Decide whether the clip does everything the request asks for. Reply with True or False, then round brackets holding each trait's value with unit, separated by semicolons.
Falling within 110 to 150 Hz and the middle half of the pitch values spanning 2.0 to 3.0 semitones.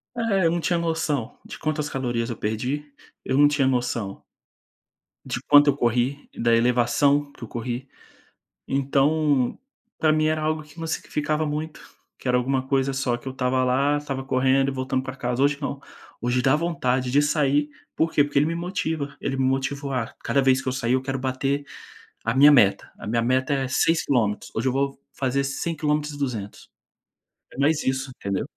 True (135 Hz; 2.6 semitones)